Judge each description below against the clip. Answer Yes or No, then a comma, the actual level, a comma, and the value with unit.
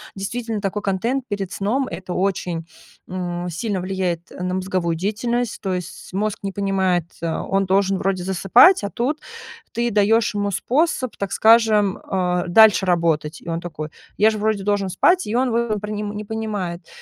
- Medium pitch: No, high, 195 Hz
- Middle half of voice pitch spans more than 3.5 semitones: No, average, 3.2 semitones